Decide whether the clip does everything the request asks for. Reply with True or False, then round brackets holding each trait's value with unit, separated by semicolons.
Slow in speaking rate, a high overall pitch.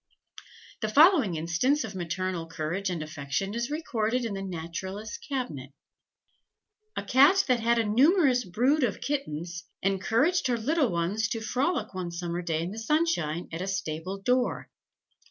False (155 wpm; 210 Hz)